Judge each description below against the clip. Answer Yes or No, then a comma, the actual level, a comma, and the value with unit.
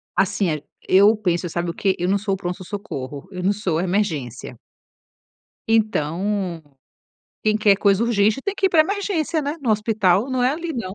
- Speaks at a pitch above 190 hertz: Yes, high, 200 Hz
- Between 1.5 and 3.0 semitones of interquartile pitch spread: No, average, 4.2 semitones